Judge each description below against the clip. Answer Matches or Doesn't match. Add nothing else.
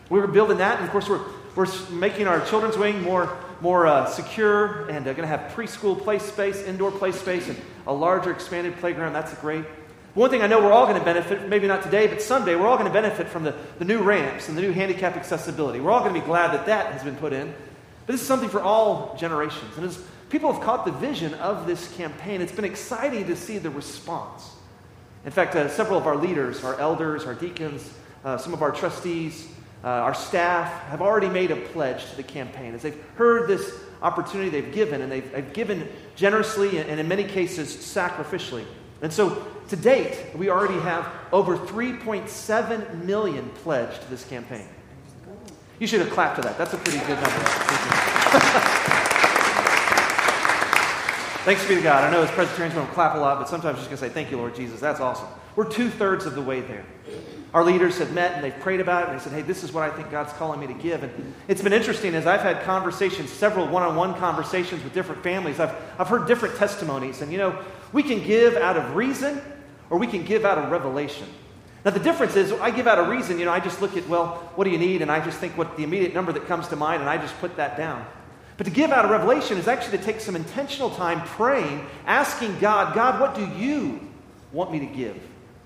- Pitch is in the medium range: Matches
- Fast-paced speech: Matches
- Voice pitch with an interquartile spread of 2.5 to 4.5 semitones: Doesn't match